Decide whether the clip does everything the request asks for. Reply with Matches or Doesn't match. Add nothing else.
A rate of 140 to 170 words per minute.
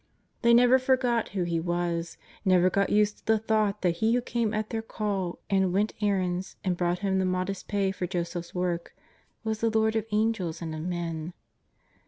Doesn't match